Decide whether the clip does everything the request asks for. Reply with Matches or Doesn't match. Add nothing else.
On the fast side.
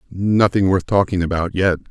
Doesn't match